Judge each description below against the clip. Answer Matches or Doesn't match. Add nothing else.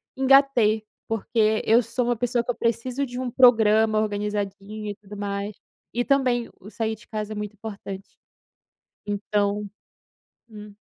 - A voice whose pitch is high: Matches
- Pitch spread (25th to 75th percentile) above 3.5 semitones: Doesn't match